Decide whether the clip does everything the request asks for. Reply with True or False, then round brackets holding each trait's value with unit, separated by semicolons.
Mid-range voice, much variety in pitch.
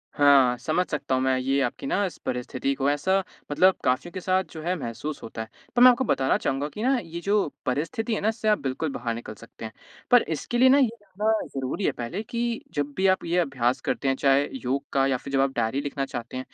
True (145 Hz; 6.4 semitones)